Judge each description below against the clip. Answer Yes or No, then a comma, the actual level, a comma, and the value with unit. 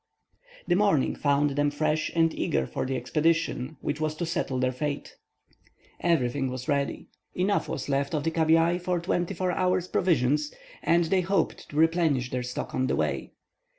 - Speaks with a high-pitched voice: No, medium, 155 Hz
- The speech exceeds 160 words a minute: Yes, average, 175 wpm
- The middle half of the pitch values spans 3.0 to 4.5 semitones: Yes, average, 3.8 semitones